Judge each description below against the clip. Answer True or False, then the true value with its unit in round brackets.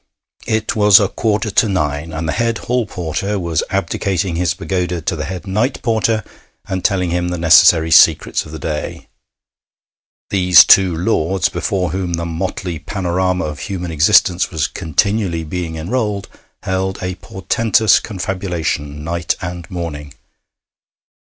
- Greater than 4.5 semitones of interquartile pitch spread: False (3.1 semitones)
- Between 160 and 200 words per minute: False (145 wpm)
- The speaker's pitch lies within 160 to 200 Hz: False (90 Hz)